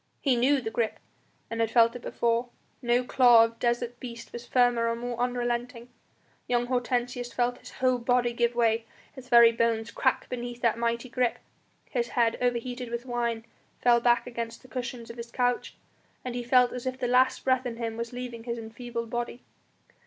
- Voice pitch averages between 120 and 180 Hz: No, high, 240 Hz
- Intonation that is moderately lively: No, narrow, 1.0 semitones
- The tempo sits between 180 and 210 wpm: Yes, average, 190 wpm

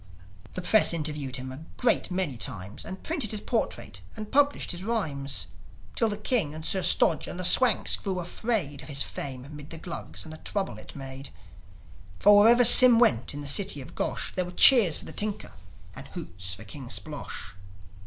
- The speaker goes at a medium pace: Yes, average, 195 wpm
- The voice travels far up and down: Yes, wide, 7.2 semitones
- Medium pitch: Yes, medium, 170 Hz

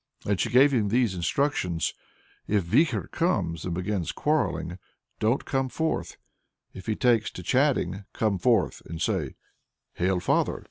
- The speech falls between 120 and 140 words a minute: No, average, 150 wpm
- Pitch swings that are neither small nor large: No, wide, 6.2 semitones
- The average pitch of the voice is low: Yes, low, 105 Hz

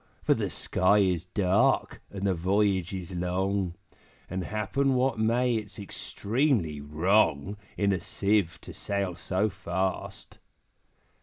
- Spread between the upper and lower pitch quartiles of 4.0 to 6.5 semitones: No, average, 2.7 semitones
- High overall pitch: No, very low, 95 Hz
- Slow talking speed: Yes, slow, 130 wpm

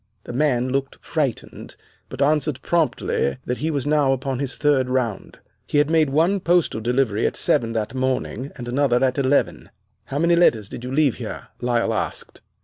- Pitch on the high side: No, low, 135 Hz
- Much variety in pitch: No, average, 3.4 semitones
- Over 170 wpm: Yes, average, 180 wpm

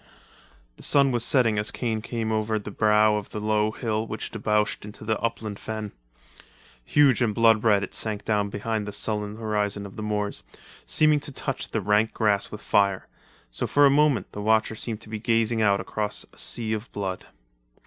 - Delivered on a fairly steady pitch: Yes, narrow, 1.5 semitones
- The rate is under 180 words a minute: No, average, 195 wpm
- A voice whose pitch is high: No, low, 110 Hz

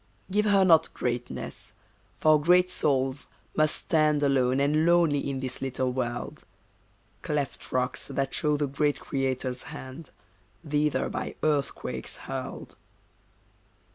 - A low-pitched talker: No, medium, 145 Hz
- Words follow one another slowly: Yes, slow, 120 wpm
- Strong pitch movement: No, average, 2.8 semitones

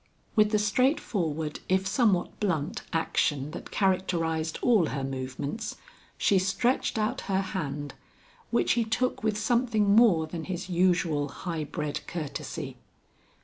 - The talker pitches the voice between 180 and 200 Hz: Yes, medium, 185 Hz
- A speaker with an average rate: No, slow, 130 wpm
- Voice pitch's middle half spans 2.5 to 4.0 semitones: No, average, 5.2 semitones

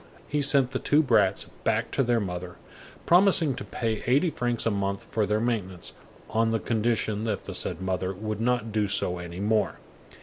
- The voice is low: Yes, low, 110 Hz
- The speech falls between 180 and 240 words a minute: Yes, average, 190 wpm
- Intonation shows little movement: No, average, 3.7 semitones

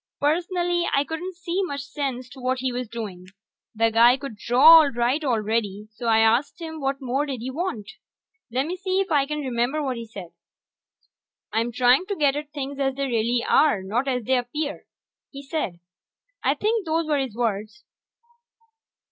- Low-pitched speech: No, very high, 265 Hz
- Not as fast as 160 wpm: No, average, 180 wpm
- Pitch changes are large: No, average, 4.4 semitones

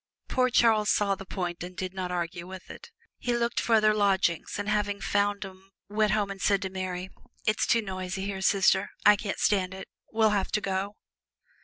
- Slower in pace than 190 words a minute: No, average, 195 wpm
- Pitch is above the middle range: Yes, high, 200 Hz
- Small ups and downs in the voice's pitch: Yes, narrow, 1.9 semitones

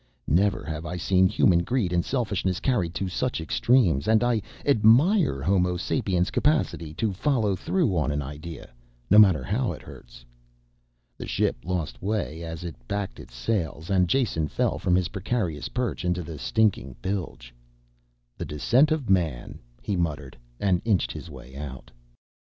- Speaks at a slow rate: No, average, 160 wpm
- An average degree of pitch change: No, wide, 5.7 semitones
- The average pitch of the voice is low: Yes, very low, 90 Hz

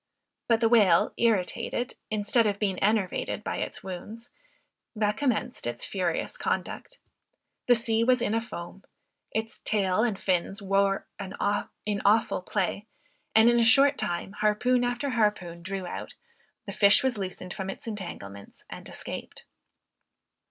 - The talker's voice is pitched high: Yes, high, 210 Hz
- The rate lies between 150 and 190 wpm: No, average, 140 wpm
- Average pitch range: Yes, average, 3.3 semitones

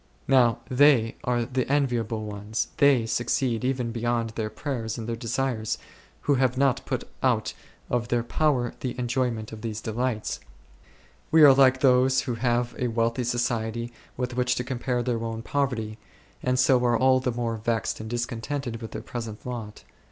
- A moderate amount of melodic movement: No, narrow, 2.1 semitones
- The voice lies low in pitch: Yes, low, 120 Hz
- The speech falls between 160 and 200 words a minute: Yes, average, 170 wpm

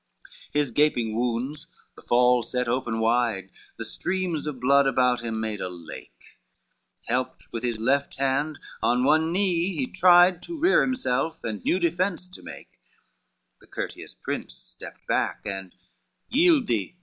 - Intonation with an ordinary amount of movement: No, wide, 6.5 semitones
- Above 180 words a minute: No, average, 155 wpm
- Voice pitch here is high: No, low, 135 Hz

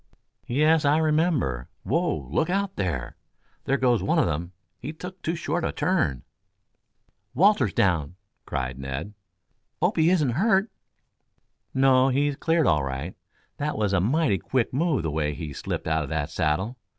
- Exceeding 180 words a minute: No, average, 160 wpm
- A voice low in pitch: Yes, low, 130 Hz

